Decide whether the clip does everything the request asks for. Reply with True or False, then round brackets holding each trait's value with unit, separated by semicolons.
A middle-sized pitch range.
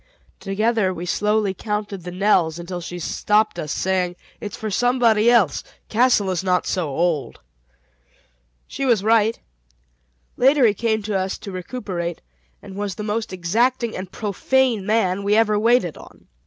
True (3.5 semitones)